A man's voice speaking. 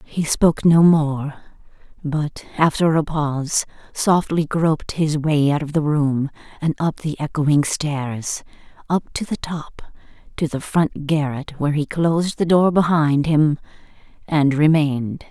No: female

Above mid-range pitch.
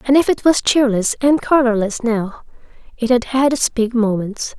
Yes: high, 245 Hz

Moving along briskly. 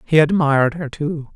No: average, 175 wpm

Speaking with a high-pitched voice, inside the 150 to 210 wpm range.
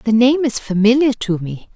Yes: high, 230 Hz; fast, 205 wpm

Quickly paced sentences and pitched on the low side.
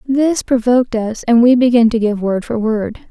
No: fast, 215 wpm; high, 235 Hz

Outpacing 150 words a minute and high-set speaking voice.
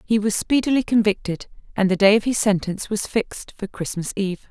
Yes: average, 200 wpm; high, 205 Hz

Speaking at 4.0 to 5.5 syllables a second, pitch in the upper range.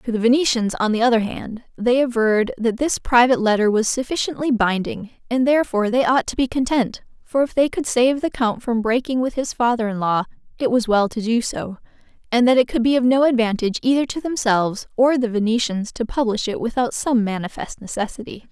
No: 5.8 syllables/s; high, 235 Hz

